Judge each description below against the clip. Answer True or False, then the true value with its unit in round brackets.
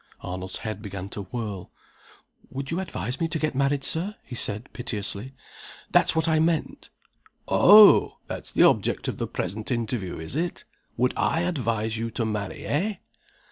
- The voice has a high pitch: False (120 Hz)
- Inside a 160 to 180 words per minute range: True (165 wpm)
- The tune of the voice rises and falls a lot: True (7.1 semitones)